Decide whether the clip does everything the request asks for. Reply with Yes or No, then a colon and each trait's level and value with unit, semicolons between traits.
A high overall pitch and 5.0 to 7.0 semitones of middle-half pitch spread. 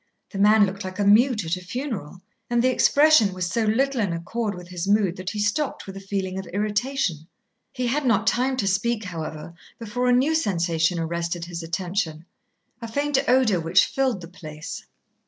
Yes: high, 200 Hz; wide, 5.4 semitones